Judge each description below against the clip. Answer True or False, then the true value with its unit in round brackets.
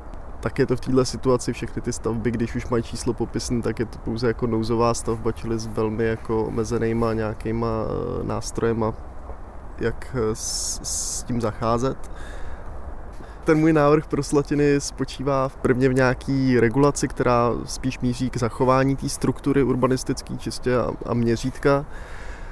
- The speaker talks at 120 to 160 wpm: True (150 wpm)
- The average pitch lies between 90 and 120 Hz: True (115 Hz)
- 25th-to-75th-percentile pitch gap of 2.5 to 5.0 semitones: True (2.8 semitones)